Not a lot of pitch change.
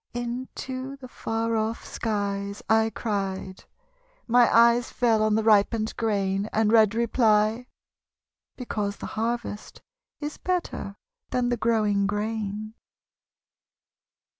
Yes: narrow, 2.3 semitones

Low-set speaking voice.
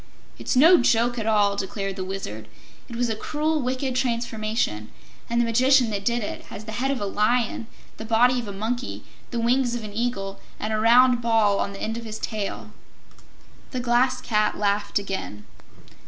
No: high, 230 Hz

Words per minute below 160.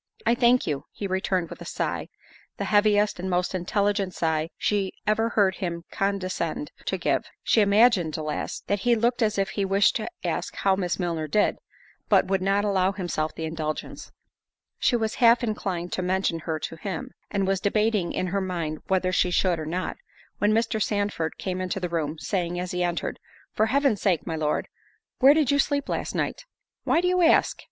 No: average, 195 wpm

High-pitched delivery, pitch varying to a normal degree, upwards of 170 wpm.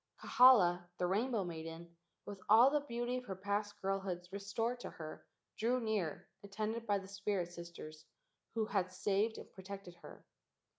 No: high, 200 Hz; average, 4.0 semitones; average, 160 wpm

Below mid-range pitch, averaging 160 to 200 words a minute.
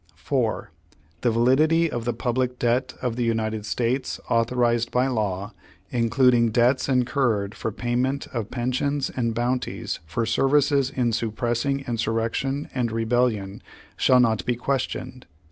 No: low, 120 Hz; slow, 135 wpm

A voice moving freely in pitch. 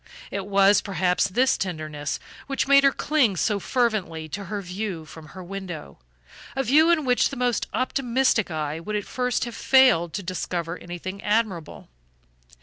Yes: wide, 6.2 semitones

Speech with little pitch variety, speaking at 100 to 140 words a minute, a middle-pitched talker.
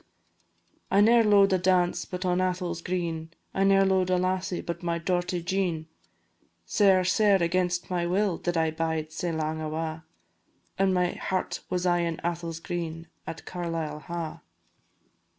No: narrow, 2.0 semitones; average, 155 wpm; medium, 175 Hz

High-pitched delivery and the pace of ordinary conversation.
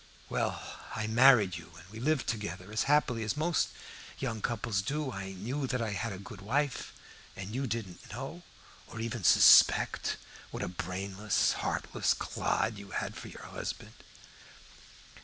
No: low, 110 Hz; average, 160 wpm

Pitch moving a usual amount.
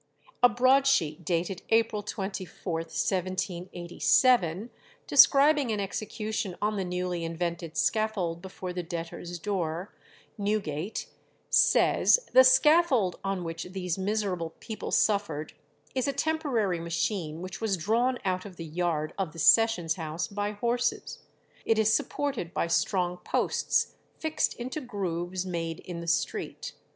Yes: average, 4.6 semitones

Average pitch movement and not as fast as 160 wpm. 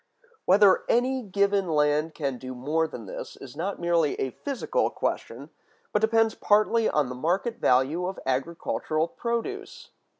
No: wide, 6.4 semitones; average, 145 wpm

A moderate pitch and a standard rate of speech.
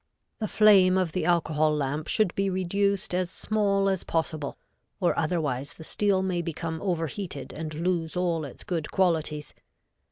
Yes: medium, 175 Hz; average, 155 wpm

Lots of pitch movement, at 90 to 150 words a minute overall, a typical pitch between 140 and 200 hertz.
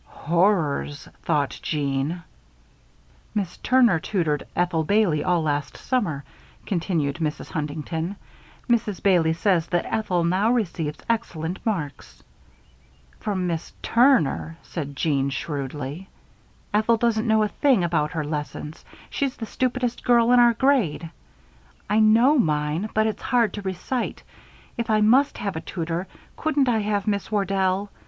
Yes: wide, 5.7 semitones; slow, 135 wpm; medium, 185 Hz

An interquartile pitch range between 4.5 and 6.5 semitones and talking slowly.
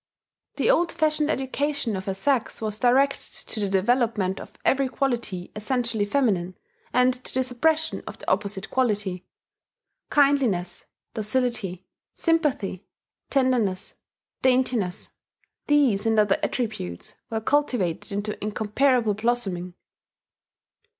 Yes: average, 4.9 semitones; slow, 110 wpm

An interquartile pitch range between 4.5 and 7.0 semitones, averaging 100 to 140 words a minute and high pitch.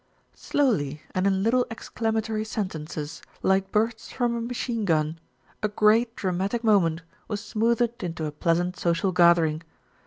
Yes: average, 5.1 semitones; slow, 135 wpm; high, 200 Hz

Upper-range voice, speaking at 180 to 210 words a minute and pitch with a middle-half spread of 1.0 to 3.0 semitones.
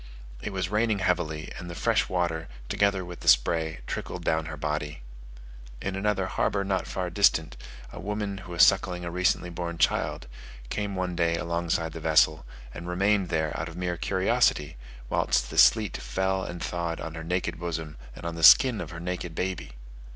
No: very low, 85 Hz; average, 185 wpm; narrow, 2.6 semitones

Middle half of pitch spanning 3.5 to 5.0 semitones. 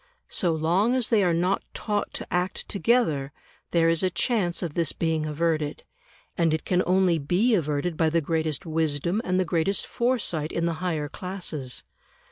No: average, 2.9 semitones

